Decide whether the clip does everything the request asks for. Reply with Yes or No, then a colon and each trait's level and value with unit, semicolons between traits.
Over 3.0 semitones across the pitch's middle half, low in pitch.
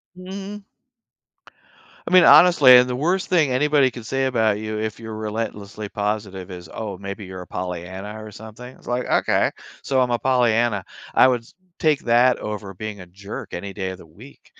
Yes: average, 4.3 semitones; low, 110 Hz